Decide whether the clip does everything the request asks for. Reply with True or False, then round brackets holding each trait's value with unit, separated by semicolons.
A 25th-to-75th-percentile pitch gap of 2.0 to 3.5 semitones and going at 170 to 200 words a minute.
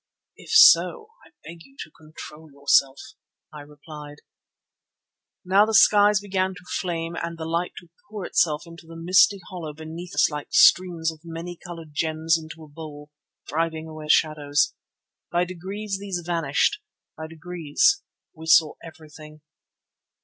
False (2.6 semitones; 150 wpm)